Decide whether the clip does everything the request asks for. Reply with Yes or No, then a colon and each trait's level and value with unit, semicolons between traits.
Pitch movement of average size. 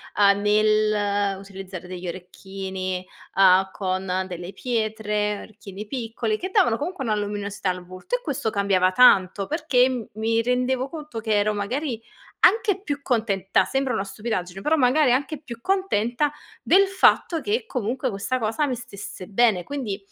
Yes: average, 4.8 semitones